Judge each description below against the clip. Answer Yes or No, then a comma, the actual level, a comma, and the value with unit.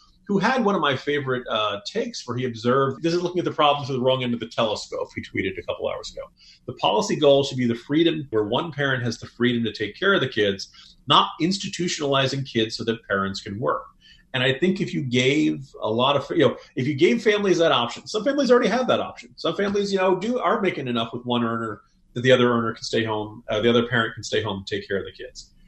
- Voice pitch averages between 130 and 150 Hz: Yes, low, 135 Hz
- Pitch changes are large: Yes, wide, 7.7 semitones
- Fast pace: Yes, fast, 260 wpm